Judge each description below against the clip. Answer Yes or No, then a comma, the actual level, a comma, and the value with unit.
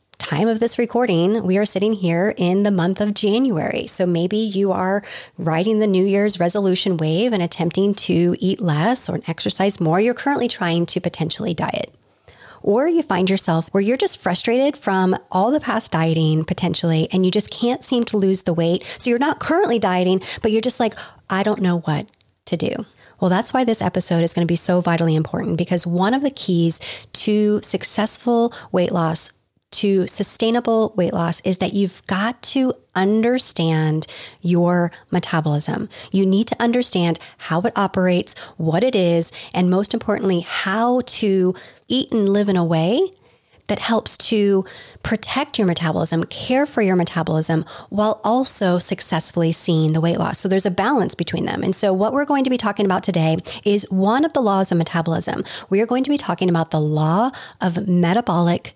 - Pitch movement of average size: Yes, average, 4.4 semitones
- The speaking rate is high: No, average, 185 wpm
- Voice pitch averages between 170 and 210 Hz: Yes, high, 190 Hz